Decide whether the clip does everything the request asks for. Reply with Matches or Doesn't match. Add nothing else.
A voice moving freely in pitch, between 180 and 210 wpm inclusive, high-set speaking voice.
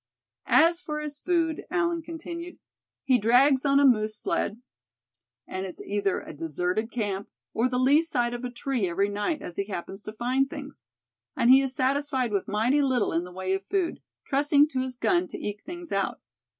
Matches